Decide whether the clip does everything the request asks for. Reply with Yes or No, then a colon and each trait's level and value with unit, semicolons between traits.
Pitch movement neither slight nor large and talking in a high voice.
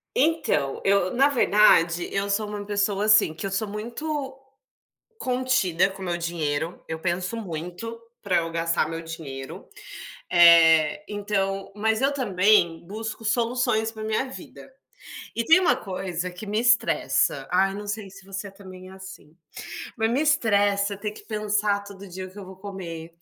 Yes: average, 3.5 semitones; high, 200 Hz